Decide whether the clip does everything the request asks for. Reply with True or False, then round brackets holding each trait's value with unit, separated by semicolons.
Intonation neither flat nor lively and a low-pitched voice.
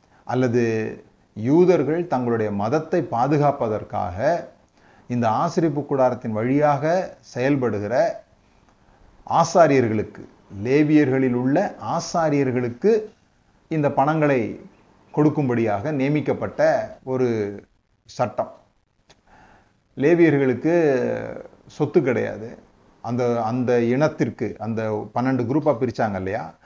True (4.6 semitones; 130 Hz)